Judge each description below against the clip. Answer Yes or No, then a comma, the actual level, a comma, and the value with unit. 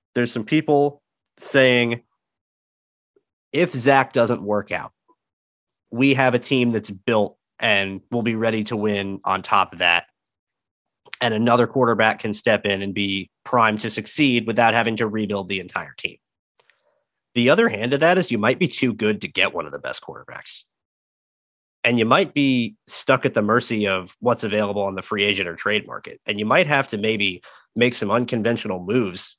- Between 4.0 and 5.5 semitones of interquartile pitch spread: No, average, 3.3 semitones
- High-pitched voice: No, low, 115 Hz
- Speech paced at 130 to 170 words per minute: No, average, 180 wpm